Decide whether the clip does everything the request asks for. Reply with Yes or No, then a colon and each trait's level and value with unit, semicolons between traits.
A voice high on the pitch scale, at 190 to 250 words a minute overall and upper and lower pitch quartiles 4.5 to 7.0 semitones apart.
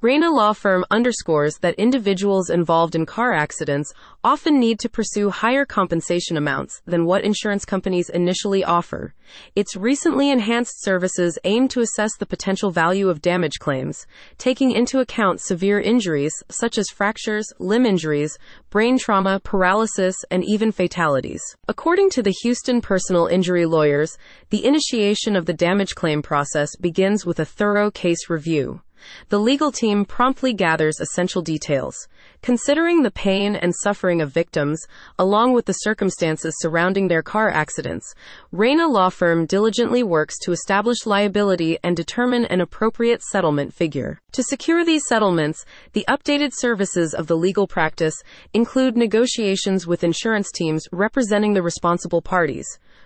No: high, 195 Hz; average, 145 wpm; average, 4.9 semitones